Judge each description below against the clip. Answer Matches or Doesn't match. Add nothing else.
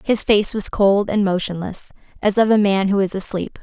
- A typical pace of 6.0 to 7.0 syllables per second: Doesn't match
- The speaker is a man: Doesn't match